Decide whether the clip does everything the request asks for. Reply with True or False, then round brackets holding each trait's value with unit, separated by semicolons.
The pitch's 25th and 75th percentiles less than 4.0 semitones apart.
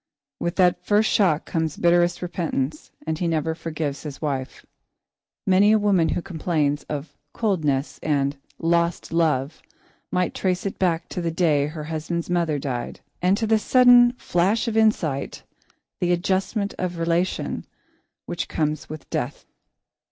True (3.3 semitones)